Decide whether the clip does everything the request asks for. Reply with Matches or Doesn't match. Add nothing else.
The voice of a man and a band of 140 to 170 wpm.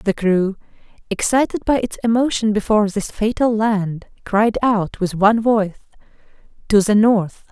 Doesn't match